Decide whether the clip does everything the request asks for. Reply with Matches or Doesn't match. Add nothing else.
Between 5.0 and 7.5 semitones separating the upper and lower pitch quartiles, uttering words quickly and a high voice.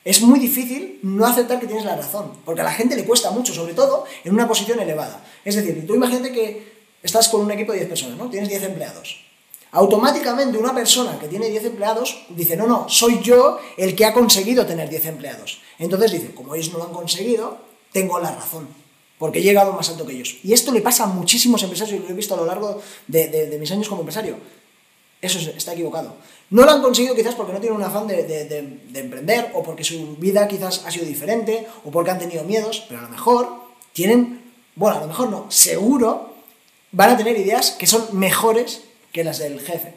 Matches